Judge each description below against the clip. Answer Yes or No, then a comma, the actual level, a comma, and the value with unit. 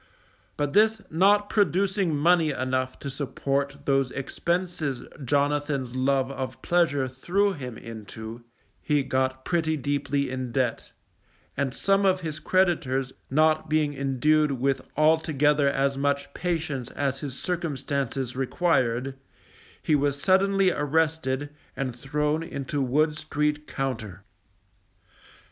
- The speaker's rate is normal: No, slow, 120 wpm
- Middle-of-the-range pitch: Yes, medium, 145 Hz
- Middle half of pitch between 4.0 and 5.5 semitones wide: No, average, 3.2 semitones